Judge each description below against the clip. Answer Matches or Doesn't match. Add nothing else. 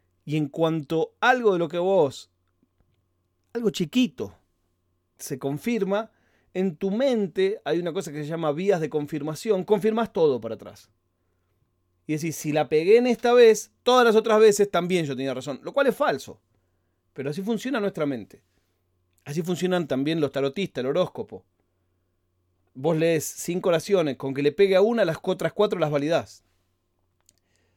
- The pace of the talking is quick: Doesn't match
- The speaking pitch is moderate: Matches